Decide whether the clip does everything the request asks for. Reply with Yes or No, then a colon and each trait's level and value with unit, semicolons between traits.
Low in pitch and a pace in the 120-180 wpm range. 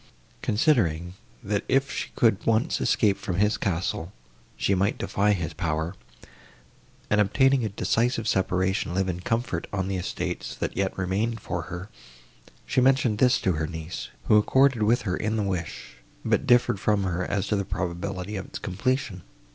Yes: low, 100 Hz; average, 170 wpm